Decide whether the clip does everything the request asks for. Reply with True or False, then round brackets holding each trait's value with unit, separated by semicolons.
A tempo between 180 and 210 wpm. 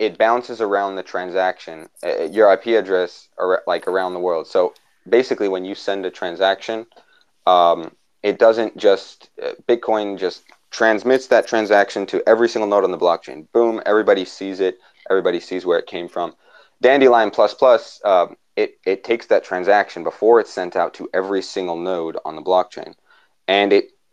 False (170 wpm)